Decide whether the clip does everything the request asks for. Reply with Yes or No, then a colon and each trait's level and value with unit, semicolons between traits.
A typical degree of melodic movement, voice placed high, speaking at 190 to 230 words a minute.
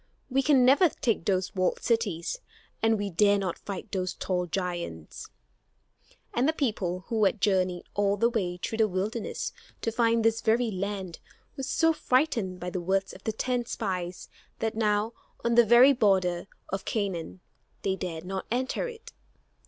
No: average, 4.2 semitones; high, 205 Hz; average, 170 wpm